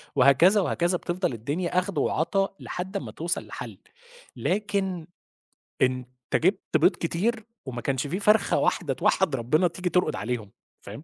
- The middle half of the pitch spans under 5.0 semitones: No, wide, 5.6 semitones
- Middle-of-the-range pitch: Yes, medium, 175 Hz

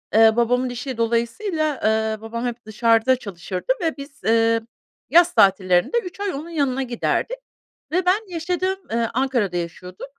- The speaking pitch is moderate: No, high, 245 Hz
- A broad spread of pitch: Yes, wide, 6.3 semitones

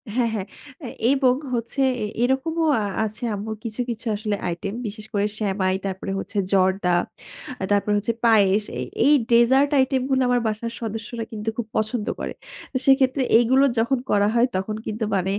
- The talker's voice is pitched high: Yes, high, 220 Hz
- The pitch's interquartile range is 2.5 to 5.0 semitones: Yes, average, 3.4 semitones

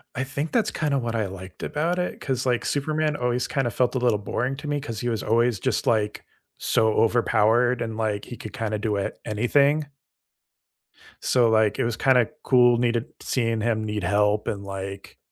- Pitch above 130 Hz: No, low, 120 Hz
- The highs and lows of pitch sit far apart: No, average, 3.5 semitones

